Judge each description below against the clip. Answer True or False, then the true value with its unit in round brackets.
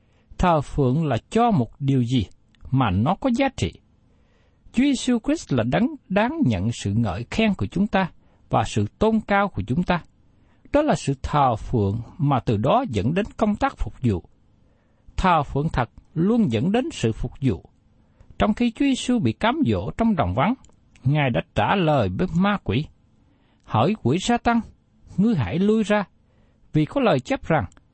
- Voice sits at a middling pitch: True (160 Hz)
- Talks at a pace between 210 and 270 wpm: False (185 wpm)